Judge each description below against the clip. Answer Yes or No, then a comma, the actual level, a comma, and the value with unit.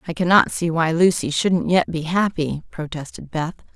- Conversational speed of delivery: Yes, average, 175 wpm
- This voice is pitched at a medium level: Yes, medium, 165 Hz